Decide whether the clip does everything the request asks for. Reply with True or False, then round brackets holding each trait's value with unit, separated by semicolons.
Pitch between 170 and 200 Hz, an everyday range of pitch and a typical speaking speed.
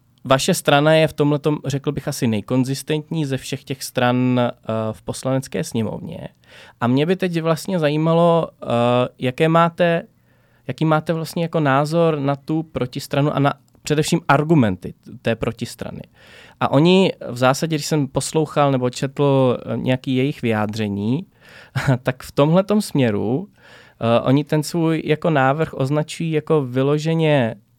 False (140 Hz; 3.8 semitones; 135 wpm)